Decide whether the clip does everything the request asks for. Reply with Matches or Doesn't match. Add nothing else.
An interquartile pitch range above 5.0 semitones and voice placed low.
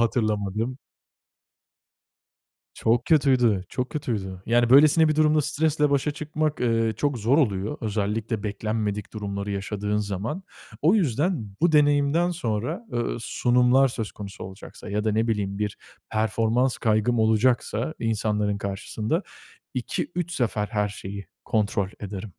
Matches